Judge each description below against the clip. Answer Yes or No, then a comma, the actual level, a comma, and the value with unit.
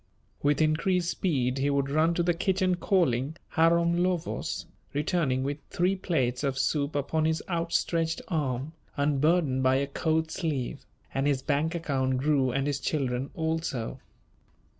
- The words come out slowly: No, average, 145 wpm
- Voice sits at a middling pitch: Yes, medium, 150 Hz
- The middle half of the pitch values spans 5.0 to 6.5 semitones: No, average, 3.6 semitones